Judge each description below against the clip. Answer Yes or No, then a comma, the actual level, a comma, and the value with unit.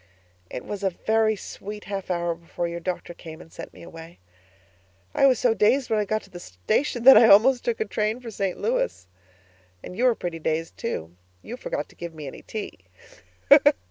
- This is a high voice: Yes, high, 200 Hz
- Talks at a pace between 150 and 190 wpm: No, fast, 205 wpm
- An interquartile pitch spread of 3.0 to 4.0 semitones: No, average, 5.0 semitones